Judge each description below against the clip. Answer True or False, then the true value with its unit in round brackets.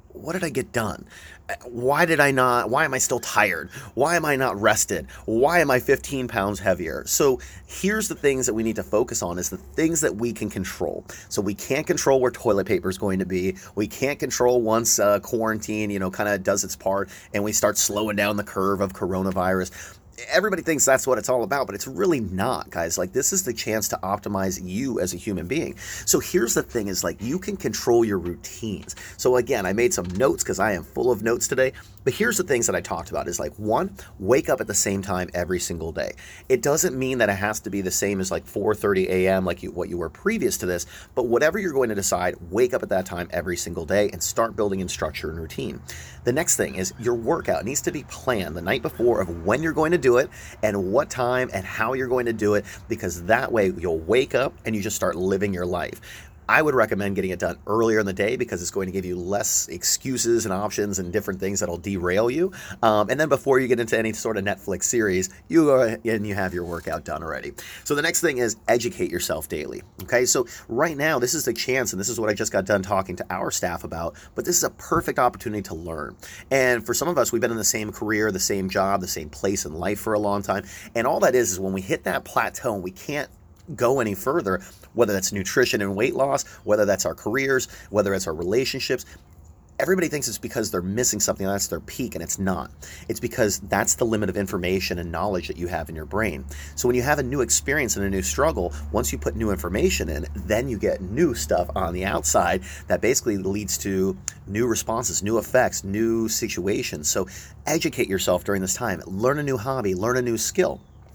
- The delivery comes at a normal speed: False (240 wpm)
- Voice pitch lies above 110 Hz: False (100 Hz)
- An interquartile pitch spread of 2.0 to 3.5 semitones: False (4.2 semitones)